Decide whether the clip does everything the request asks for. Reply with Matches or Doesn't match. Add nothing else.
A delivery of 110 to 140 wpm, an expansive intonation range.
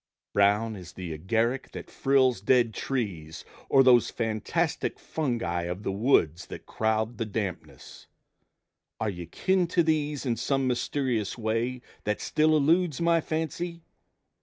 Matches